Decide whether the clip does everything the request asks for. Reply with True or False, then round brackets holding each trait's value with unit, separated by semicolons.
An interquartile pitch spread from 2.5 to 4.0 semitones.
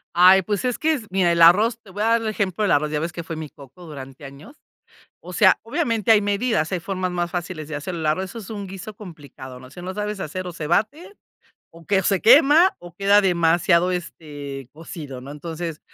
False (4.7 semitones)